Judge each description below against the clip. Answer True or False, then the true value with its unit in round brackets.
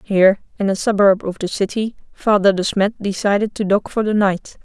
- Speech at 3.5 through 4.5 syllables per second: False (5.4 syllables/s)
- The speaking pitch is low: False (200 Hz)